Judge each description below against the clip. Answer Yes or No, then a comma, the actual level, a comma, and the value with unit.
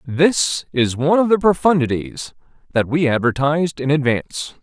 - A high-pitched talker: No, medium, 150 Hz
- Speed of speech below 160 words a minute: Yes, average, 145 wpm